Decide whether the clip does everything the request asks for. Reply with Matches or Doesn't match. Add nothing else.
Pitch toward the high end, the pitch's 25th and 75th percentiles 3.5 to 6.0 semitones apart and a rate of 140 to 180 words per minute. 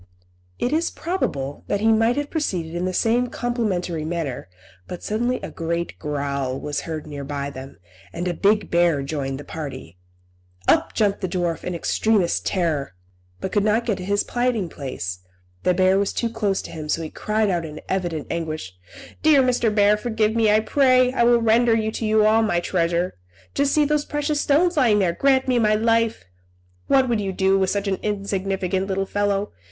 Doesn't match